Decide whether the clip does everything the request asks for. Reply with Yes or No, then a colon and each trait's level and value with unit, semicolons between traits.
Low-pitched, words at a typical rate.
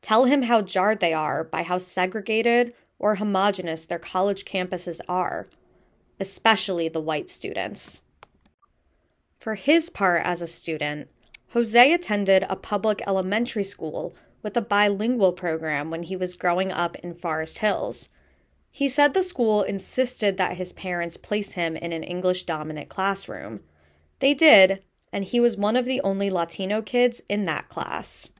No: high, 195 Hz; average, 150 wpm